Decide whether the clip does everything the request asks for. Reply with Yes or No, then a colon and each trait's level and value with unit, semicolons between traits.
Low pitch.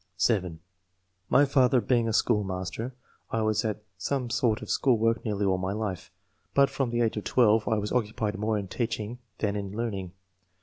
Yes: low, 110 Hz